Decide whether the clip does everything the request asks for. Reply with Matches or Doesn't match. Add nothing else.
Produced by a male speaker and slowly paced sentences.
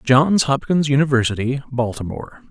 Matches